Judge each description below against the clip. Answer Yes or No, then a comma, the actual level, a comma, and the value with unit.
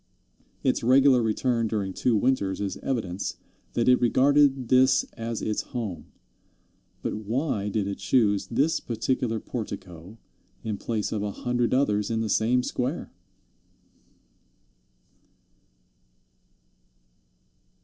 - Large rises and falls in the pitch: No, average, 3.7 semitones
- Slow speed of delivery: Yes, slow, 110 wpm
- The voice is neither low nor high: No, low, 115 Hz